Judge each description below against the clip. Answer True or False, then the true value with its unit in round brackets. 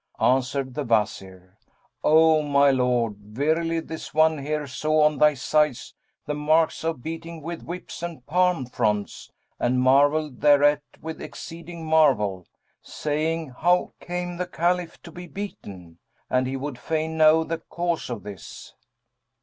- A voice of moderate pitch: True (150 Hz)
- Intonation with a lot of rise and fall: False (4.2 semitones)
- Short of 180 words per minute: True (140 wpm)